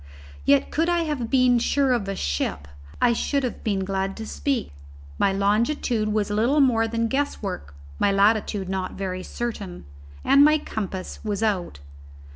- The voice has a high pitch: Yes, high, 215 Hz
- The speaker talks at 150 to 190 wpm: Yes, average, 160 wpm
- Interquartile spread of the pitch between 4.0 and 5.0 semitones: Yes, average, 4.6 semitones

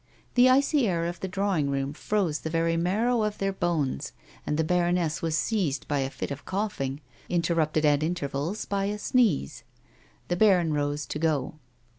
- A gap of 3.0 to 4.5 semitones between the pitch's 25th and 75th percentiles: No, average, 4.9 semitones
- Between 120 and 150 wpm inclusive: No, average, 175 wpm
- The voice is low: No, medium, 170 Hz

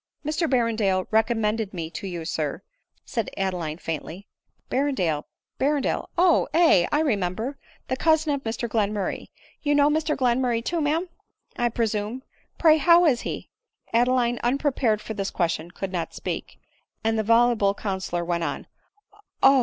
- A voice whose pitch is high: Yes, high, 230 Hz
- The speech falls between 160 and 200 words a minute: Yes, average, 170 wpm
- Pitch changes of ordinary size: No, wide, 6.5 semitones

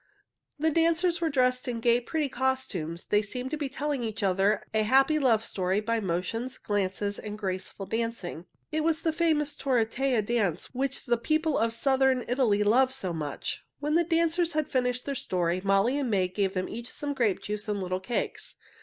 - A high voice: Yes, high, 240 Hz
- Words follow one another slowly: No, average, 190 wpm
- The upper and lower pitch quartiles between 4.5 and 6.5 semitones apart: Yes, wide, 5.5 semitones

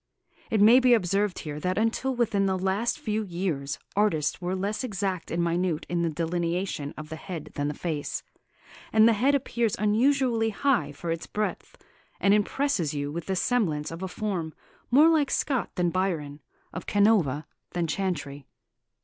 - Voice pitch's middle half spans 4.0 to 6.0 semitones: Yes, average, 4.9 semitones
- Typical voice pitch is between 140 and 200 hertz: Yes, high, 190 Hz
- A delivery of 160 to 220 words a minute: Yes, average, 170 wpm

